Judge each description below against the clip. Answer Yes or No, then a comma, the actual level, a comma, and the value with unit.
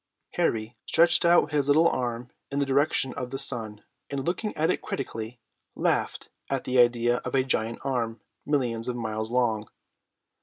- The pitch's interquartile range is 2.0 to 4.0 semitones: Yes, average, 3.4 semitones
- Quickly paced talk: No, average, 165 wpm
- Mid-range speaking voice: No, low, 125 Hz